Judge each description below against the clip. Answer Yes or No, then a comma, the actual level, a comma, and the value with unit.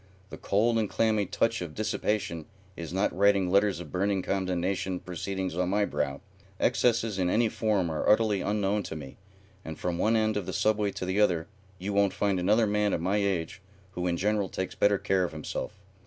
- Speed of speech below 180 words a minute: No, average, 200 wpm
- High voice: No, low, 100 Hz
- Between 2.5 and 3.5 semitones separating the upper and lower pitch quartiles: Yes, average, 2.8 semitones